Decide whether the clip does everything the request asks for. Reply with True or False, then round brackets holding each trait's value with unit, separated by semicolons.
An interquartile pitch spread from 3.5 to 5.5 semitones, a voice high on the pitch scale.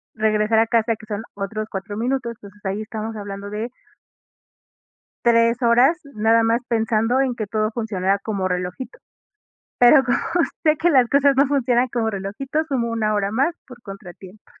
False (3.0 semitones; 225 Hz)